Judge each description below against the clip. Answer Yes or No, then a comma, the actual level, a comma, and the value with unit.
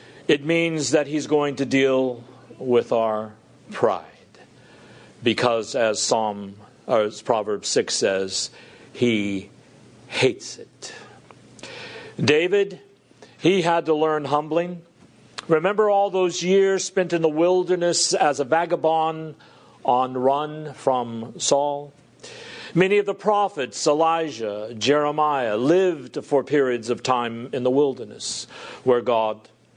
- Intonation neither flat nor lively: No, wide, 5.7 semitones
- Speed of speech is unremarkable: No, slow, 115 wpm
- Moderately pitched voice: Yes, medium, 145 Hz